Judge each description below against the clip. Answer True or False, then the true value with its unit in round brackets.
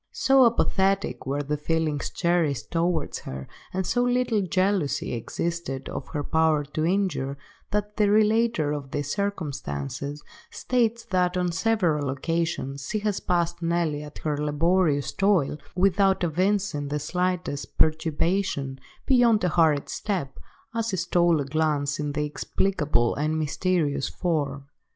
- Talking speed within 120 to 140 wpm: True (135 wpm)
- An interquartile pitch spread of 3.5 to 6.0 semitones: True (4.7 semitones)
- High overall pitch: False (165 Hz)